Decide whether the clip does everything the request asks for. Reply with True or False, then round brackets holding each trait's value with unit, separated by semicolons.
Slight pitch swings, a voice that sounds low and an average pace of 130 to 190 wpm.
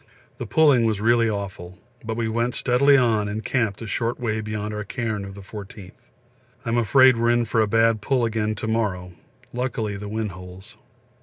False (2.3 semitones; 110 Hz; 200 wpm)